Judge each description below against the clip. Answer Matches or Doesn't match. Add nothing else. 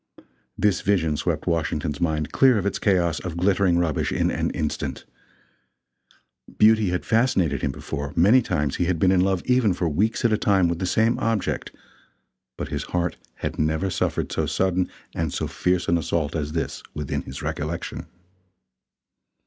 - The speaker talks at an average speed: Matches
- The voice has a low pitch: Matches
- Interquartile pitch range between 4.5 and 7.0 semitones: Doesn't match